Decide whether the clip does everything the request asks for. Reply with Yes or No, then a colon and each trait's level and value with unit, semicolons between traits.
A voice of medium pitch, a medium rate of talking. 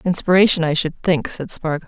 Yes: medium, 170 Hz; average, 190 wpm